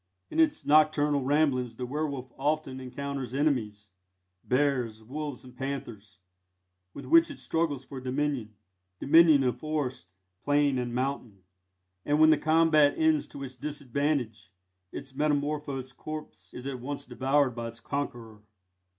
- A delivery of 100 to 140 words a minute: Yes, slow, 135 wpm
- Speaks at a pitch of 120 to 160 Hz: Yes, medium, 140 Hz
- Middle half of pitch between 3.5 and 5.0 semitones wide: No, average, 2.9 semitones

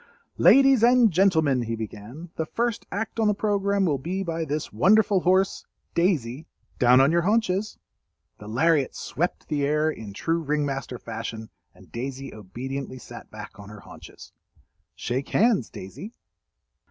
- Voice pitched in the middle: Yes, medium, 155 Hz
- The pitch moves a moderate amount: No, wide, 7.4 semitones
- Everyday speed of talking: Yes, average, 150 wpm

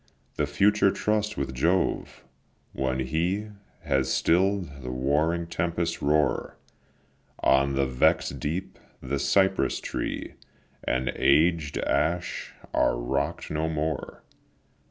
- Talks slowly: Yes, slow, 110 wpm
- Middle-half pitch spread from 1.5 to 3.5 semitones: No, average, 4.4 semitones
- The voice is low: Yes, very low, 75 Hz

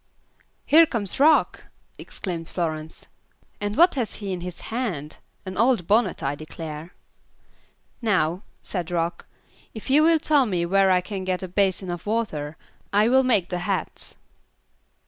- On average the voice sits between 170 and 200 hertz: Yes, high, 190 Hz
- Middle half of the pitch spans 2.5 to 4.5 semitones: No, average, 5.1 semitones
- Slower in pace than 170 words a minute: Yes, average, 150 wpm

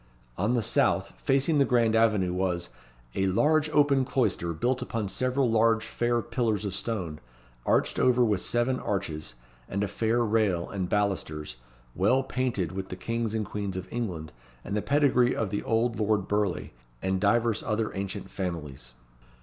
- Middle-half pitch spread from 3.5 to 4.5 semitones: Yes, average, 4.1 semitones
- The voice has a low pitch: Yes, low, 105 Hz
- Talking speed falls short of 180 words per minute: Yes, average, 165 wpm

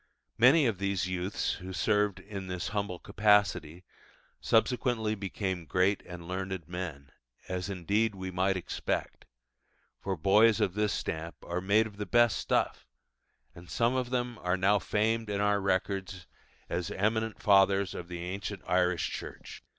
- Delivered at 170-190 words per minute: No, average, 150 wpm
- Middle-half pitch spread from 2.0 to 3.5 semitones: Yes, narrow, 2.5 semitones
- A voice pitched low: Yes, very low, 95 Hz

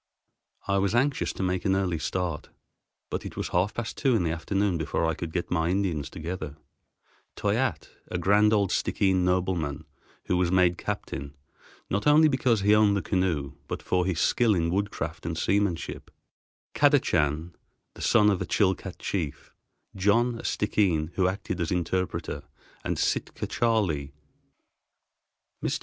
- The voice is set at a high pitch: No, very low, 95 Hz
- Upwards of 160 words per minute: No, average, 155 wpm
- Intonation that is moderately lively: Yes, average, 3.6 semitones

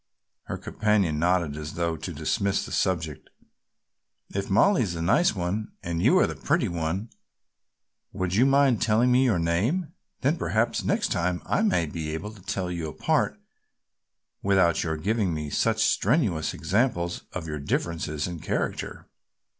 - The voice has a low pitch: Yes, very low, 90 Hz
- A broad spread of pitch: No, average, 4.4 semitones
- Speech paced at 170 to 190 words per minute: No, average, 155 wpm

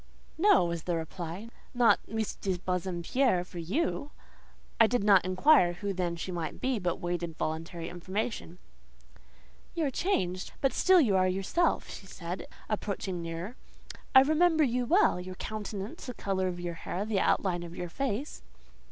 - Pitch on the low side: No, high, 190 Hz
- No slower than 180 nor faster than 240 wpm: No, average, 160 wpm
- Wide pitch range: Yes, wide, 5.8 semitones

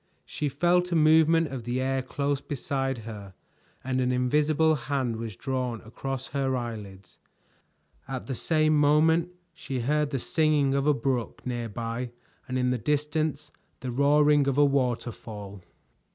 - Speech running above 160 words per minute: No, average, 150 wpm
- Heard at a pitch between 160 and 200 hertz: No, low, 135 Hz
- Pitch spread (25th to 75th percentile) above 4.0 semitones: No, average, 3.4 semitones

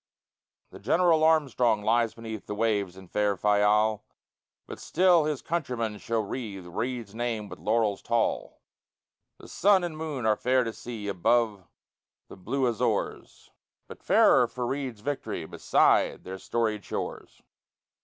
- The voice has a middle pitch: No, low, 115 Hz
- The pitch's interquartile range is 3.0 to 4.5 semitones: Yes, average, 3.8 semitones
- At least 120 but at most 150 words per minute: Yes, average, 140 wpm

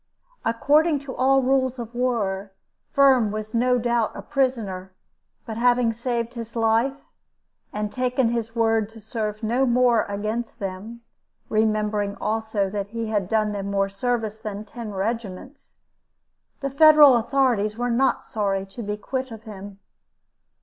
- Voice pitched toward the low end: No, high, 225 Hz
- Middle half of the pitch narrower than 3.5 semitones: Yes, average, 3.0 semitones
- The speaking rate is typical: Yes, average, 145 wpm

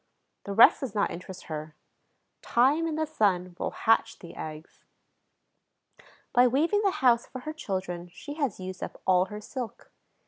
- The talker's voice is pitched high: Yes, high, 215 Hz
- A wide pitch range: Yes, wide, 7.0 semitones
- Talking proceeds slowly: No, average, 165 wpm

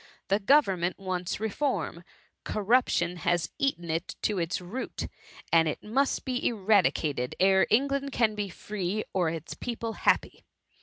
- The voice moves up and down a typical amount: Yes, average, 4.9 semitones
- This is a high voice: Yes, high, 195 Hz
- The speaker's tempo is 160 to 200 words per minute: No, slow, 135 wpm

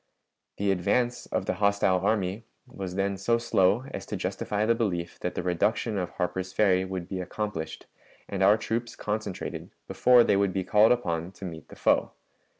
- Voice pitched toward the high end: No, low, 100 Hz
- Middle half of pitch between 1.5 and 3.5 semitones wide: Yes, average, 2.9 semitones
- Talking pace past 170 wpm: Yes, average, 180 wpm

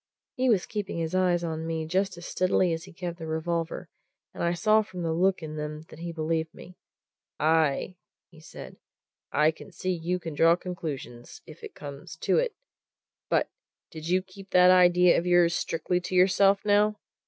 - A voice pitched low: No, medium, 175 Hz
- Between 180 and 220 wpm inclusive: Yes, average, 185 wpm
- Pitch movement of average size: No, narrow, 2.3 semitones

